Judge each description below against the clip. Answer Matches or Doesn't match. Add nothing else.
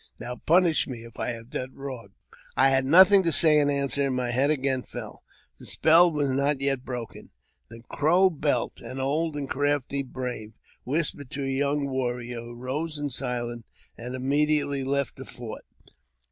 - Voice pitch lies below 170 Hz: Matches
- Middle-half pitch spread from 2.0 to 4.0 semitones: Matches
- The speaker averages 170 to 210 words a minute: Matches